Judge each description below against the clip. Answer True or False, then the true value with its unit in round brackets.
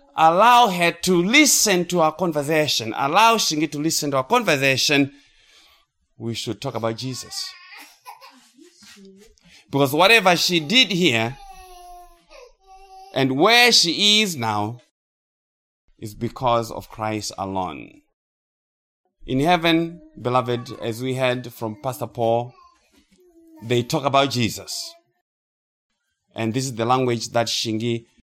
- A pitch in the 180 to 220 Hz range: False (140 Hz)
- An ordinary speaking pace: False (115 wpm)